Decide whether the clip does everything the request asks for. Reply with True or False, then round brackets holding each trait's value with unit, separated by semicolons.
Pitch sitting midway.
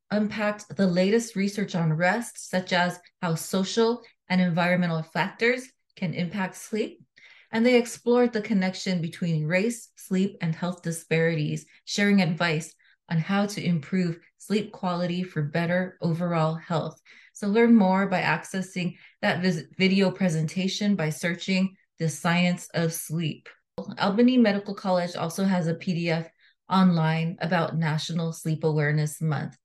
True (180 Hz)